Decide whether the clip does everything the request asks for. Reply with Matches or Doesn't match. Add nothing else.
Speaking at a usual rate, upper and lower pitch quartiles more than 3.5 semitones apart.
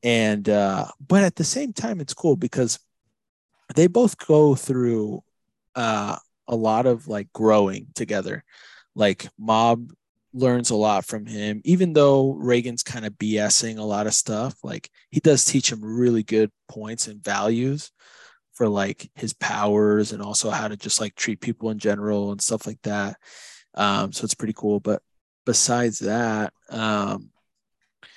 Matches